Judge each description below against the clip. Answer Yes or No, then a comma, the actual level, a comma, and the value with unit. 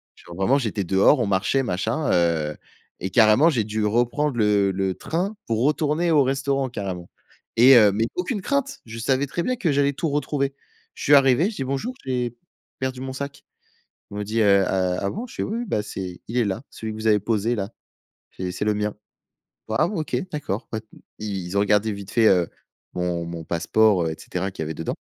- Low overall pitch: Yes, low, 110 Hz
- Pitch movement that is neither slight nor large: No, wide, 6.1 semitones